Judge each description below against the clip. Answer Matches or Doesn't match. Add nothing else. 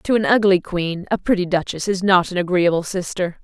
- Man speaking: Doesn't match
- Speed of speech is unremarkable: Doesn't match